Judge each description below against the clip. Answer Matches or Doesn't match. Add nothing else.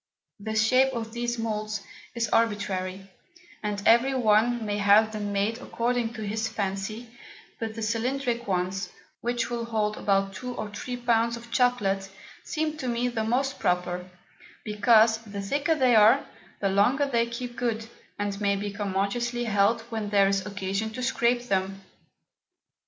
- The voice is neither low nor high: Doesn't match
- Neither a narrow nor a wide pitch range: Matches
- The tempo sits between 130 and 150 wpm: Doesn't match